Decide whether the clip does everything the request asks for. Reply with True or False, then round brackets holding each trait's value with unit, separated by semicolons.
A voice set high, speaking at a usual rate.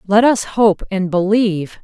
True (200 Hz; 165 wpm)